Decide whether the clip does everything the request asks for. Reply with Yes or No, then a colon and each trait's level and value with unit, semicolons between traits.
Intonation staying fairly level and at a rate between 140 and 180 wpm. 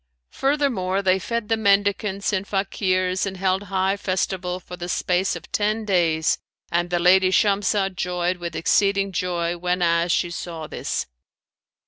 Yes: narrow, 2.0 semitones; average, 145 wpm